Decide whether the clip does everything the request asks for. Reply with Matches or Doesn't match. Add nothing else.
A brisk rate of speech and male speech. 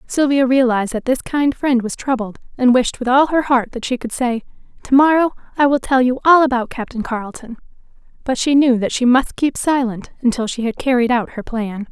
Doesn't match